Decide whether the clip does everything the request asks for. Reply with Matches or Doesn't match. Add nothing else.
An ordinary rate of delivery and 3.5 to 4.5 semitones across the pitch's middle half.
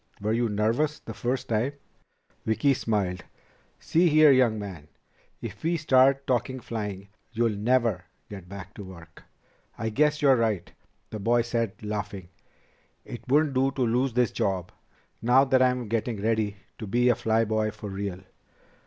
Matches